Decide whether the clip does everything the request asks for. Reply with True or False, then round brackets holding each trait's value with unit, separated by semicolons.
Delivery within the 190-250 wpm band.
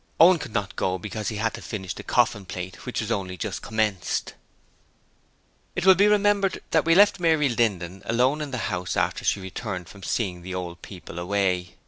True (195 wpm)